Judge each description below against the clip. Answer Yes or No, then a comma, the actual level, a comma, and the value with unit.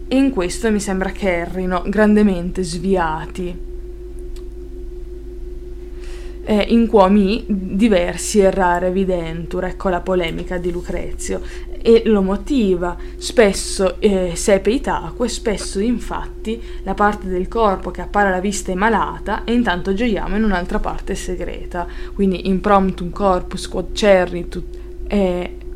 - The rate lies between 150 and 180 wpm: No, average, 125 wpm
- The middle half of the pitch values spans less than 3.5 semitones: No, average, 4.2 semitones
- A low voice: No, high, 195 Hz